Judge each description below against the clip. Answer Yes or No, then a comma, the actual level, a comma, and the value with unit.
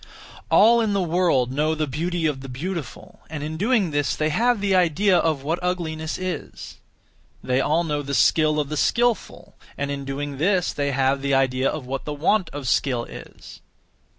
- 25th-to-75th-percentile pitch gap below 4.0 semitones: No, average, 4.3 semitones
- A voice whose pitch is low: No, medium, 155 Hz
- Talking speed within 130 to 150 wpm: No, average, 190 wpm